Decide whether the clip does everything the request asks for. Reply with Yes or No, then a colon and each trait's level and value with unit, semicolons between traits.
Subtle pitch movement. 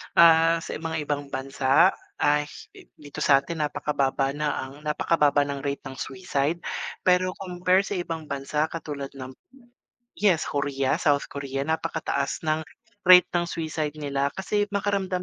No: average, 3.3 semitones